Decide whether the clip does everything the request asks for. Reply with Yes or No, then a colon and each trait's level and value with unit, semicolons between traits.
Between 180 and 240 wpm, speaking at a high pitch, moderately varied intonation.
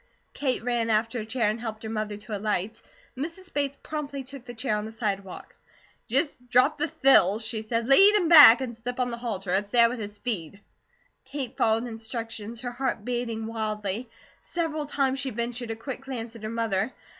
Yes: average, 195 wpm; high, 235 Hz; average, 3.3 semitones